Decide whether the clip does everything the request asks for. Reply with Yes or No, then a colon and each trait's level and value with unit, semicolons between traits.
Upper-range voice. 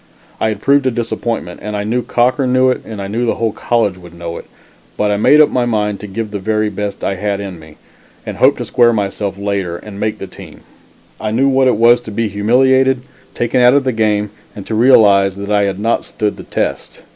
No: low, 110 Hz